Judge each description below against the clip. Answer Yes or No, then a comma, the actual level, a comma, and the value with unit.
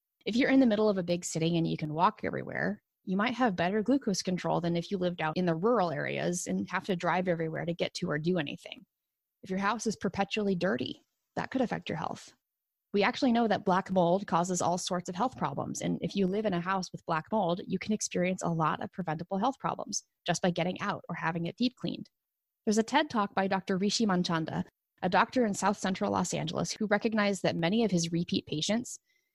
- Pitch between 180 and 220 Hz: Yes, high, 190 Hz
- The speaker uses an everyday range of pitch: Yes, average, 3.7 semitones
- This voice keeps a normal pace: No, fast, 235 wpm